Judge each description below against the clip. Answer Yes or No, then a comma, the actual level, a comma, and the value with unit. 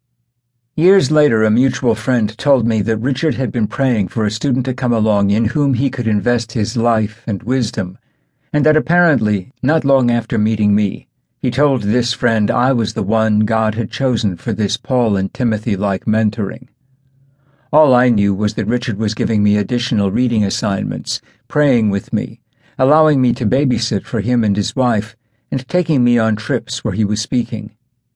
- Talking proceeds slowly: No, average, 180 wpm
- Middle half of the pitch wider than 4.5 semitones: No, average, 3.3 semitones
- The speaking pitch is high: No, low, 120 Hz